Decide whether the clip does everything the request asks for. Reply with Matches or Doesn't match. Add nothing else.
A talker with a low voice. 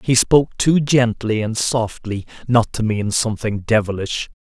Matches